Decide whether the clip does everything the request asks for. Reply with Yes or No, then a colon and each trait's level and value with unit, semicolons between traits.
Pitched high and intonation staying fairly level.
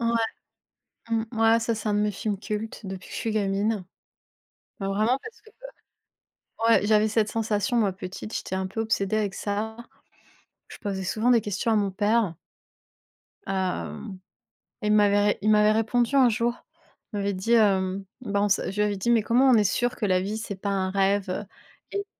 Yes: high, 210 Hz; narrow, 2.2 semitones